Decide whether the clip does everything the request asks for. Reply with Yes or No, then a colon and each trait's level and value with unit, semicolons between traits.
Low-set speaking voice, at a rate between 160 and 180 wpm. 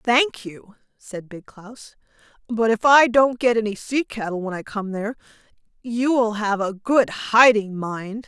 No: high, 220 Hz; average, 175 wpm